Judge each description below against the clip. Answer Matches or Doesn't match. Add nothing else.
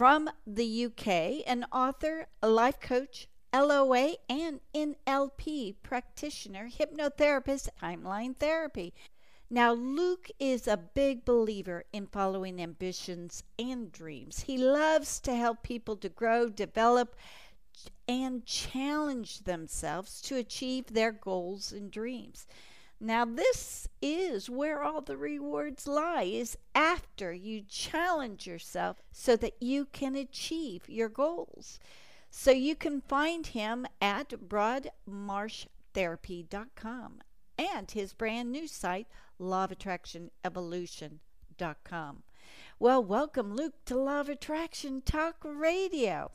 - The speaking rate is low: Matches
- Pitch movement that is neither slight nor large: Doesn't match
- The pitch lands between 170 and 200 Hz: Doesn't match